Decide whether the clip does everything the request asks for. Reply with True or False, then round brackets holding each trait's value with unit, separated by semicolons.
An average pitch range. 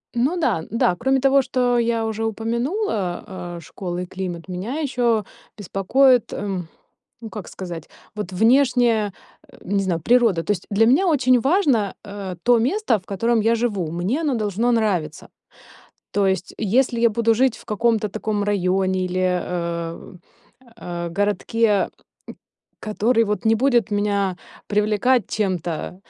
True (4.2 semitones)